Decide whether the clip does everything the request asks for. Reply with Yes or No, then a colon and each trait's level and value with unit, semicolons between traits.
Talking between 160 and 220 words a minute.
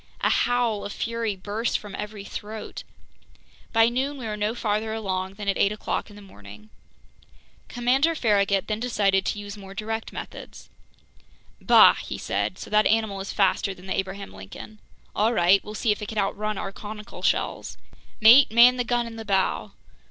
Yes: average, 180 wpm